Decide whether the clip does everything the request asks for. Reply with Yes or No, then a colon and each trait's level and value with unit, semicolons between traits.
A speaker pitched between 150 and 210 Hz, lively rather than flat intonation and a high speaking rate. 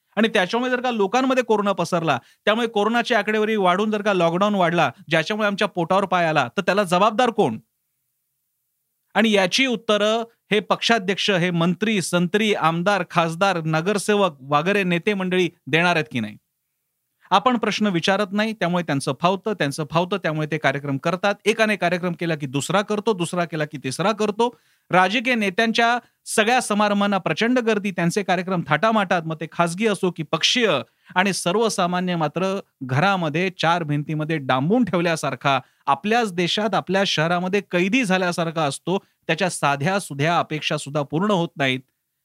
No: medium, 185 Hz; average, 4.5 semitones; fast, 150 wpm